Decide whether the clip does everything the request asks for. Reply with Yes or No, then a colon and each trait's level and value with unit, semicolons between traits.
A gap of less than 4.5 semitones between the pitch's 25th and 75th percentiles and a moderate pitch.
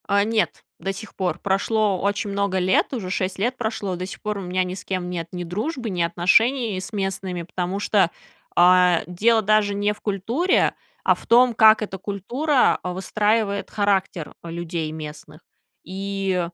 No: average, 2.9 semitones; high, 195 Hz